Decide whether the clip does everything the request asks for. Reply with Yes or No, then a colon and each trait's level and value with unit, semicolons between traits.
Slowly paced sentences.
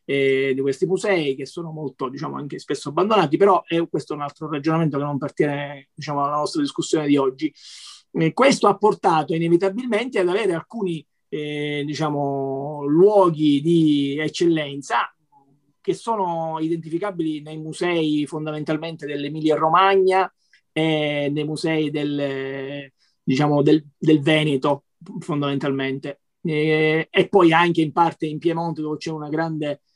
No: average, 140 wpm